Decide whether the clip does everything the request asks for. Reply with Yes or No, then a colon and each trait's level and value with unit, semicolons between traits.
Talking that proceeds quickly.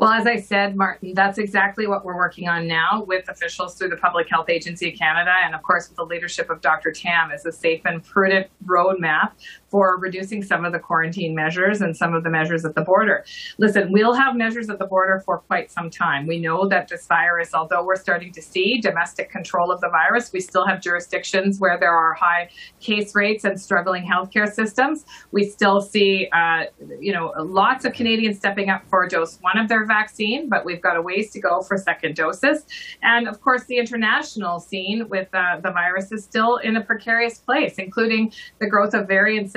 Yes: fast, 210 wpm